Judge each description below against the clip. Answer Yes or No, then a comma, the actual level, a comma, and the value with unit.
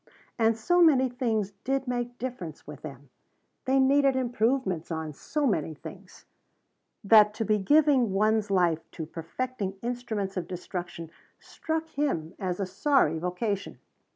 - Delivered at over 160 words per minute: No, average, 140 wpm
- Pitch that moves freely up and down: Yes, wide, 6.3 semitones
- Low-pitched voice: No, high, 215 Hz